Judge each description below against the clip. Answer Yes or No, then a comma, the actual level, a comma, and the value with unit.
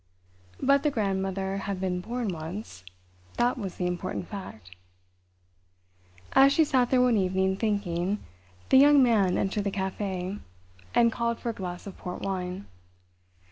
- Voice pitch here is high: Yes, high, 195 Hz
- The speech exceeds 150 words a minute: No, average, 140 wpm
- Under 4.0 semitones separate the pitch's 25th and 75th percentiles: No, average, 4.4 semitones